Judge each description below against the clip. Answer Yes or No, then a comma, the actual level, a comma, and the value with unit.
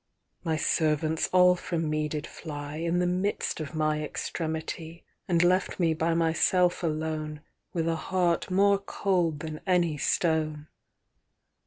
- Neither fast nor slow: No, slow, 125 wpm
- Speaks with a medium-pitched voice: Yes, medium, 165 Hz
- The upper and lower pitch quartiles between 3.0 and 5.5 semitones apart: No, narrow, 2.4 semitones